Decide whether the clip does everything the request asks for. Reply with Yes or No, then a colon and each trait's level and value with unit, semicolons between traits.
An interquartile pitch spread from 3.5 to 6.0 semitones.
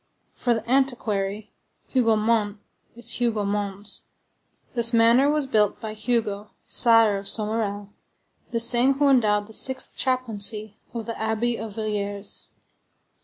No: narrow, 2.5 semitones